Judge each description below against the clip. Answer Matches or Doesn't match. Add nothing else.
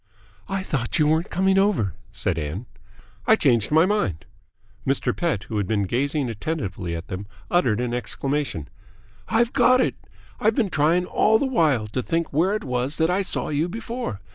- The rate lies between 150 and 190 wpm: Matches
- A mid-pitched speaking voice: Matches